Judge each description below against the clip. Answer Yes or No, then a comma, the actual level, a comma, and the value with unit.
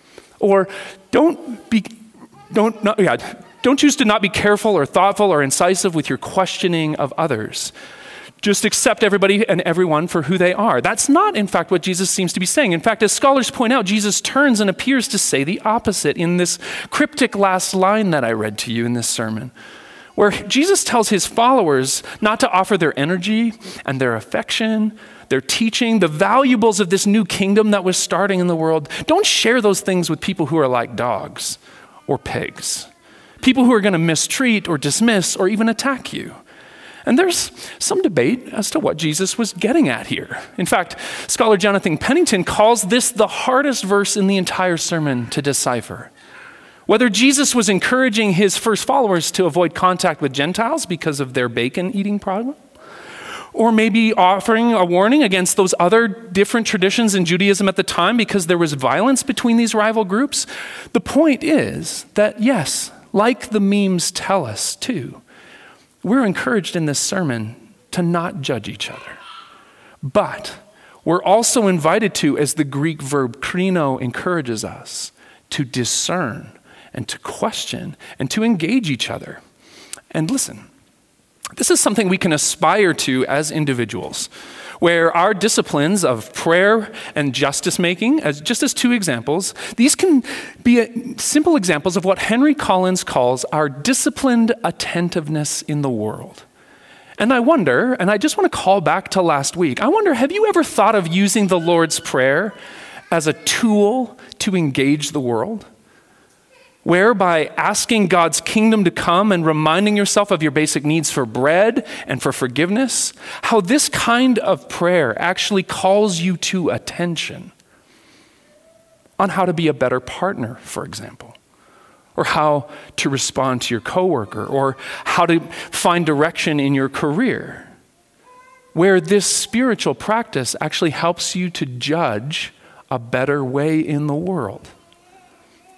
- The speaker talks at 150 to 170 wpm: Yes, average, 160 wpm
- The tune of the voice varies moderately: No, wide, 6.3 semitones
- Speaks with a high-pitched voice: Yes, high, 195 Hz